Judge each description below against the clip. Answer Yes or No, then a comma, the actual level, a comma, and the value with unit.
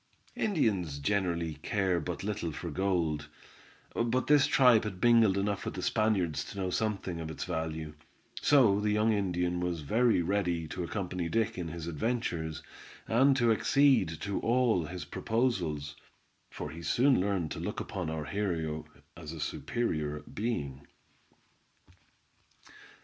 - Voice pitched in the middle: No, very low, 95 Hz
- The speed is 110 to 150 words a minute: Yes, average, 145 wpm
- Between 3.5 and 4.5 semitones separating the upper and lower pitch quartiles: No, wide, 5.5 semitones